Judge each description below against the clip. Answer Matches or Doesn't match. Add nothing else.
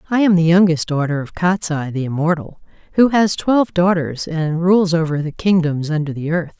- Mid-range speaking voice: Matches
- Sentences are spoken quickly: Doesn't match